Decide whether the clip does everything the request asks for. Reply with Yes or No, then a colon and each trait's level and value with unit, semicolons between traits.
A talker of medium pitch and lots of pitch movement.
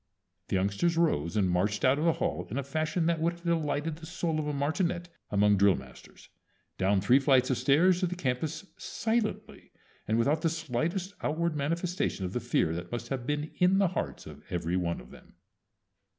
Yes: medium, 145 Hz; wide, 8.4 semitones